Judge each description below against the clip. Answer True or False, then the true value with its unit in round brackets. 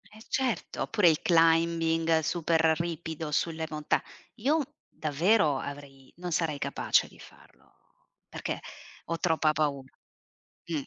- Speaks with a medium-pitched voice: True (165 Hz)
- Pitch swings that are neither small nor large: False (2.0 semitones)